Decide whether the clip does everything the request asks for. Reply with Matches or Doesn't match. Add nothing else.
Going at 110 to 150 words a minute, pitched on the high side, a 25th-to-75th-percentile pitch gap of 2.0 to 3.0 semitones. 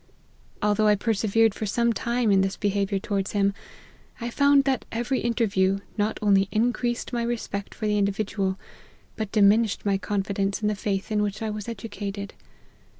Doesn't match